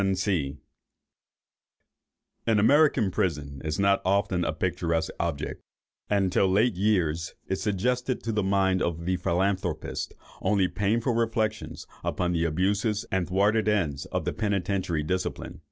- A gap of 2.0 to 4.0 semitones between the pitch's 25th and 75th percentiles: Yes, average, 3.4 semitones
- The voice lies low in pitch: Yes, very low, 95 Hz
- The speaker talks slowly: Yes, slow, 125 wpm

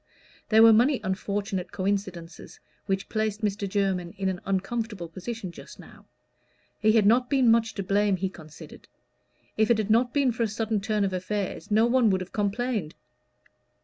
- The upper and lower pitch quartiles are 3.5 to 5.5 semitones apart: No, average, 2.9 semitones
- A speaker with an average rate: Yes, average, 175 wpm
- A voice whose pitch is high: Yes, high, 205 Hz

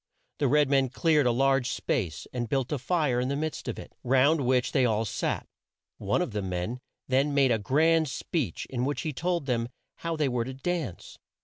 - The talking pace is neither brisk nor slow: No, fast, 210 wpm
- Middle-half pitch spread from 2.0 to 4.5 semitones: Yes, average, 3.4 semitones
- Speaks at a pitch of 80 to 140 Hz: Yes, low, 135 Hz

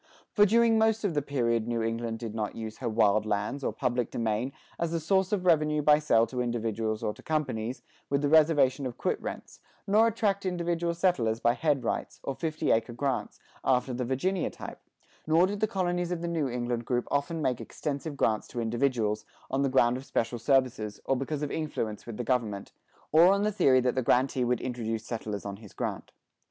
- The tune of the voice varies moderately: No, wide, 5.7 semitones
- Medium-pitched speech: No, low, 130 Hz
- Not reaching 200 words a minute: No, fast, 205 wpm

